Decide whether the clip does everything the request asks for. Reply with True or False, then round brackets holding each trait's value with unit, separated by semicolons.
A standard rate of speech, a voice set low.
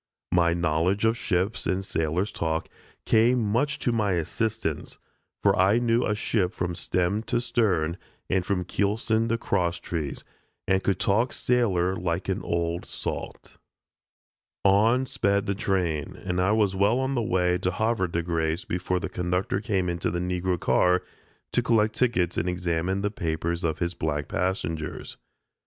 True (160 wpm; 95 Hz)